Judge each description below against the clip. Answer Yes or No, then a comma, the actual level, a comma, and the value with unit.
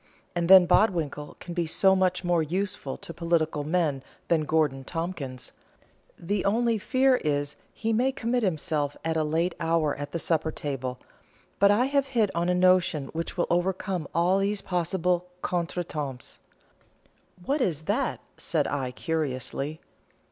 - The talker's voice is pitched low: No, medium, 170 Hz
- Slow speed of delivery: No, average, 155 wpm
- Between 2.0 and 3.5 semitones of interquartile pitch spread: No, average, 3.9 semitones